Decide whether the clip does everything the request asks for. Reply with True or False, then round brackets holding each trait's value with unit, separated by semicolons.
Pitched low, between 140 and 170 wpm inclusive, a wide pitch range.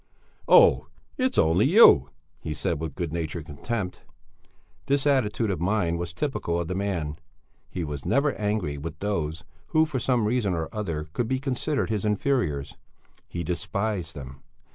True (95 Hz; 160 wpm; 6.8 semitones)